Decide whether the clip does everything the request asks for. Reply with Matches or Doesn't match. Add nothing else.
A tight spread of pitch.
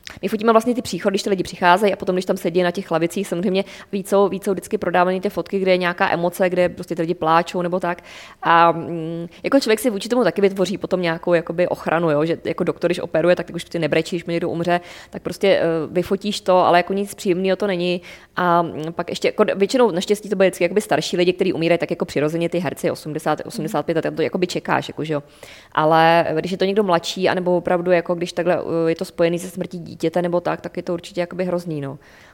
Matches